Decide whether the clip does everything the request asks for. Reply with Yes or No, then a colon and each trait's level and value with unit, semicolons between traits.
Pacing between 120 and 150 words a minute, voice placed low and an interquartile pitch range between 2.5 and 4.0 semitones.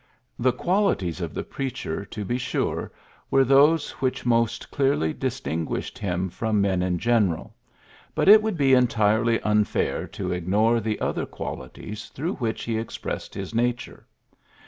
No: average, 145 wpm; low, 115 Hz; average, 4.9 semitones